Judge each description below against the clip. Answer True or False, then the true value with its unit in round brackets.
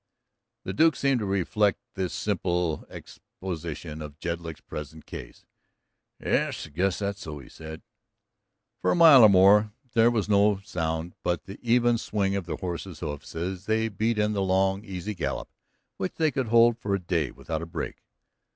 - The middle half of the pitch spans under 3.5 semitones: False (4.1 semitones)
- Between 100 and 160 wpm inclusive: False (175 wpm)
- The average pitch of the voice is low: True (95 Hz)